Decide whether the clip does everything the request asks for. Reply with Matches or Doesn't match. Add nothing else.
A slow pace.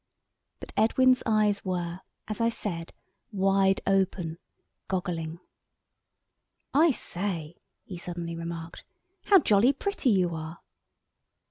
Matches